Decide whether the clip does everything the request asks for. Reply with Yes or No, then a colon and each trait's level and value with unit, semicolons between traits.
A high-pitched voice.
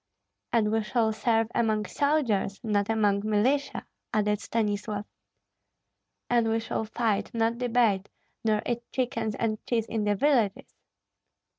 Yes: high, 220 Hz